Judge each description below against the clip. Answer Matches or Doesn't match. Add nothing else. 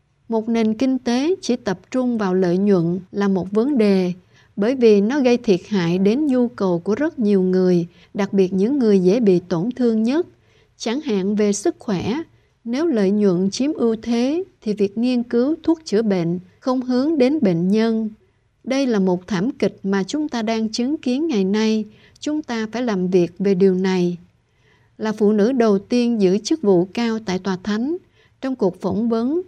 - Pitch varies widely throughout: Doesn't match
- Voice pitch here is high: Matches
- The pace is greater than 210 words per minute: Doesn't match